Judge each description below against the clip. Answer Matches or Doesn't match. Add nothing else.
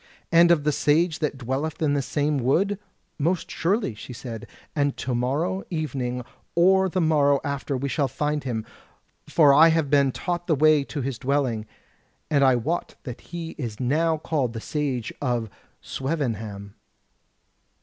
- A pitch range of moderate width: Matches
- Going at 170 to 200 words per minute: Doesn't match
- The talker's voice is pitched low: Doesn't match